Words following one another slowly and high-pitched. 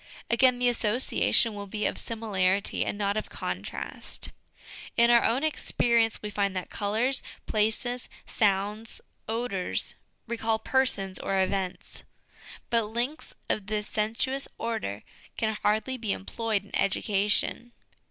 Yes: slow, 130 wpm; high, 220 Hz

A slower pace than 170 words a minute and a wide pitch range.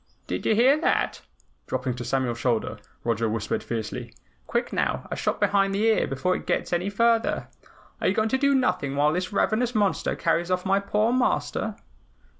No: average, 185 wpm; wide, 9.0 semitones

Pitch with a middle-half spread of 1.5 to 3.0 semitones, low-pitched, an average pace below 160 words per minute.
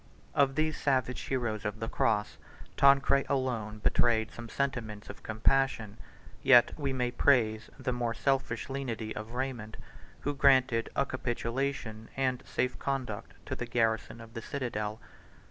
No: average, 3.4 semitones; low, 120 Hz; average, 145 wpm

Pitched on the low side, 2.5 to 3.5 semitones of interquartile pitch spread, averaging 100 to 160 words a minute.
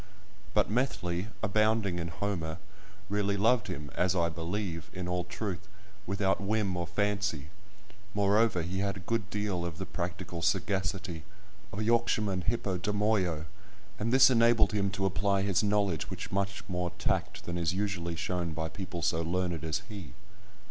Yes: very low, 95 Hz; average, 3.0 semitones; average, 155 wpm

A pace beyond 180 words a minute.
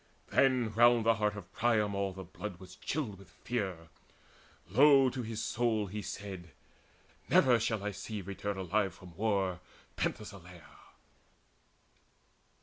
No: slow, 135 wpm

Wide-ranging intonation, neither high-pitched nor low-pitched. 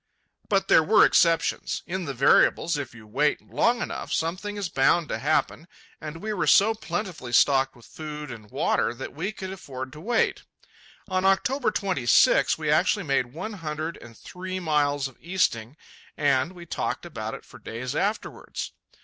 Yes: wide, 5.7 semitones; medium, 160 Hz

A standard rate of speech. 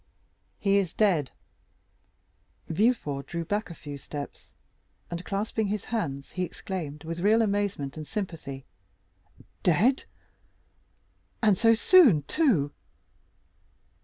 No: slow, 100 wpm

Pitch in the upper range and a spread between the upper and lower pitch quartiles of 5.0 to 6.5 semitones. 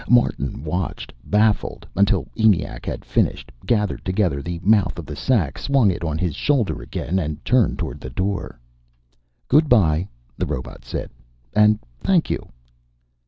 No: low, 100 Hz; wide, 5.5 semitones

